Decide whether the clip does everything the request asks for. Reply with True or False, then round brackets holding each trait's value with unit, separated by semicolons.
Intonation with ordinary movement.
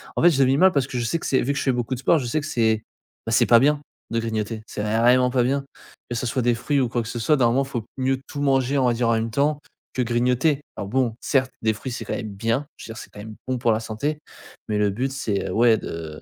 True (3.2 semitones)